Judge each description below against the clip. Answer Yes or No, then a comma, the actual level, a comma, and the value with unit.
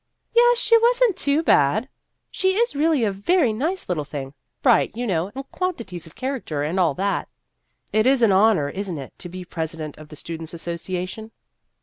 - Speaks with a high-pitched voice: Yes, high, 200 Hz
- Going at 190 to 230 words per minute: Yes, average, 200 wpm